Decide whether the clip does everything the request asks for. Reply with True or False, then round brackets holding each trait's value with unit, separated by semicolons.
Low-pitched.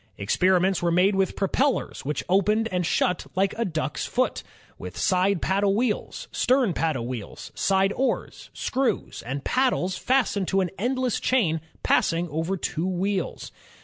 False (190 Hz)